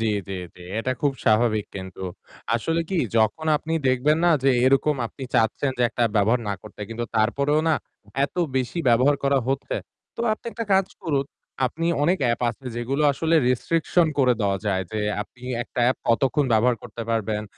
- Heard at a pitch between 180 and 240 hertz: No, low, 130 Hz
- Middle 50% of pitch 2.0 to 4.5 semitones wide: No, average, 4.9 semitones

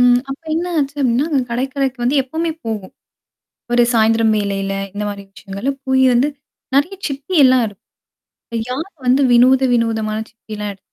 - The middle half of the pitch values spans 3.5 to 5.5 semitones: Yes, average, 3.9 semitones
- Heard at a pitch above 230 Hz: Yes, high, 245 Hz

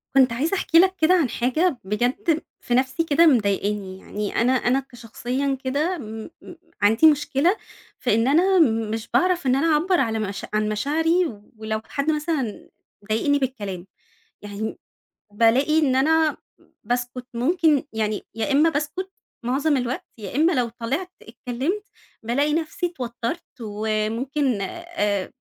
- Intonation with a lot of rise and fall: Yes, wide, 6.1 semitones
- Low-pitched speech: No, very high, 260 Hz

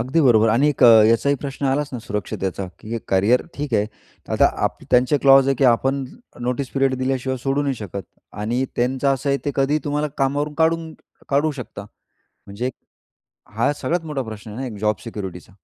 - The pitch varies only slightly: No, average, 3.9 semitones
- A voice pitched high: No, low, 130 Hz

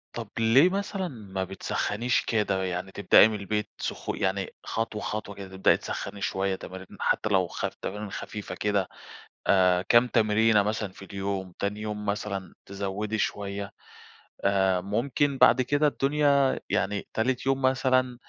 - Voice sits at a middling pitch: No, low, 105 Hz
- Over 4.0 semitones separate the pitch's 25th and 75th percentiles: No, average, 3.7 semitones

